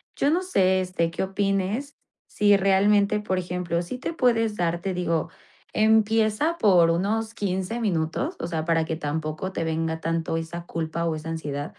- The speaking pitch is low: No, medium, 185 Hz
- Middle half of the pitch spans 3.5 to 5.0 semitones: Yes, average, 4.2 semitones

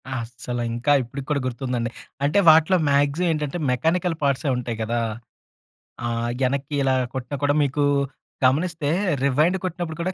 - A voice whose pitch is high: No, medium, 140 Hz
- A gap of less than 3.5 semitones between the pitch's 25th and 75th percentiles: No, average, 3.8 semitones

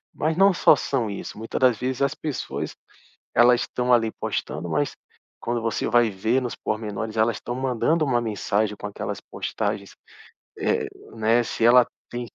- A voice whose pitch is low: Yes, low, 120 Hz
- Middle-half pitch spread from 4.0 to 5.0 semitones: No, narrow, 2.6 semitones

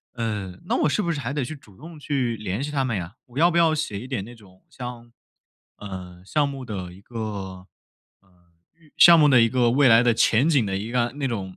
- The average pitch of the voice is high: No, low, 120 Hz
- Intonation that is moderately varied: No, wide, 5.9 semitones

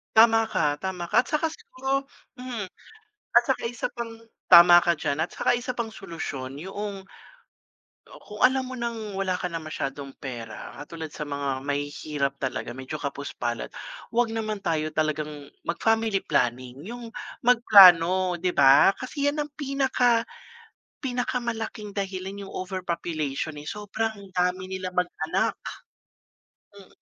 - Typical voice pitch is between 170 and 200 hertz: Yes, high, 190 Hz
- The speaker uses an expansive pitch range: Yes, wide, 6.9 semitones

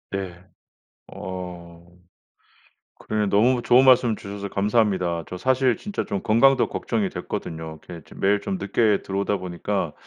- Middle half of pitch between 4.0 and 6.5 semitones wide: Yes, average, 5.1 semitones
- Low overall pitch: Yes, low, 100 Hz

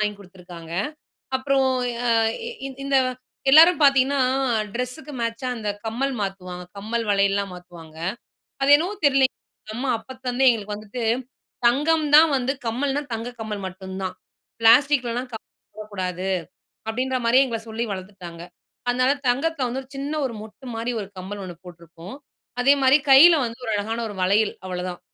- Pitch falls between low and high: No, high, 230 Hz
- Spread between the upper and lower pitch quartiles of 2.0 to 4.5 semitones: No, average, 5.2 semitones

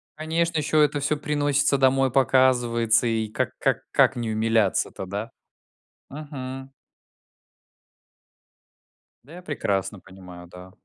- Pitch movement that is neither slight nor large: Yes, average, 5.0 semitones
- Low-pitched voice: Yes, low, 130 Hz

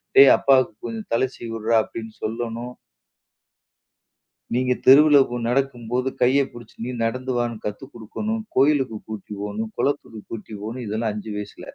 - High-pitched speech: No, low, 120 Hz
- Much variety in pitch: No, average, 3.0 semitones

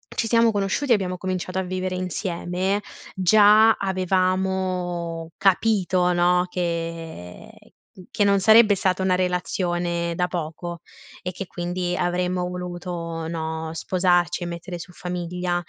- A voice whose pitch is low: No, medium, 180 Hz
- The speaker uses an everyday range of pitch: No, narrow, 1.4 semitones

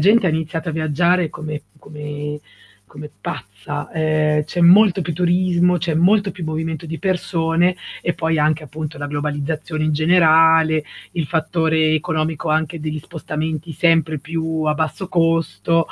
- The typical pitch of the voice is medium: Yes, medium, 160 Hz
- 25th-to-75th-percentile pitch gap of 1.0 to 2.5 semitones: Yes, narrow, 1.8 semitones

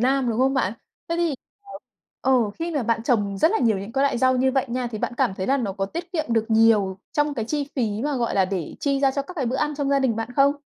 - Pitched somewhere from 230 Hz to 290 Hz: Yes, very high, 255 Hz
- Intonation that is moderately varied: Yes, average, 4.0 semitones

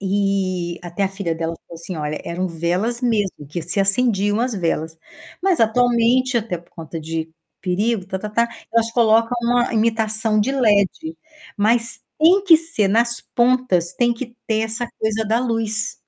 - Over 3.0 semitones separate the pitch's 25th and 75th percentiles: Yes, average, 4.3 semitones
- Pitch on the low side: No, high, 220 Hz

